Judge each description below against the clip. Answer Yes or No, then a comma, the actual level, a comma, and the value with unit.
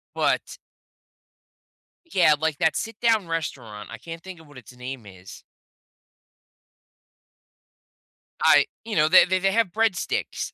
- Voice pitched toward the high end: No, medium, 165 Hz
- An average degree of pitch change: No, wide, 6.7 semitones